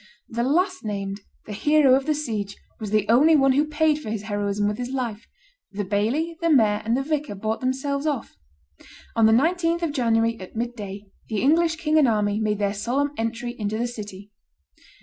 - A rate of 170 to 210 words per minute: Yes, average, 195 wpm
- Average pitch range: No, wide, 5.9 semitones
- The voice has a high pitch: Yes, high, 235 Hz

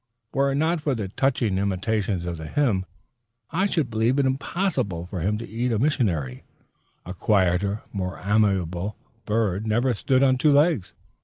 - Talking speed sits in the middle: Yes, average, 165 wpm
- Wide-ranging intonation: Yes, wide, 6.1 semitones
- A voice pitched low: Yes, low, 110 Hz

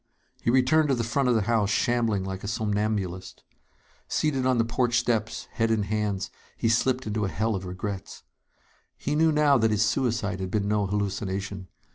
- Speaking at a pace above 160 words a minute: Yes, average, 185 wpm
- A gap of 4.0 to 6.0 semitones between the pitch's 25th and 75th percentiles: No, average, 3.2 semitones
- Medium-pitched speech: No, low, 110 Hz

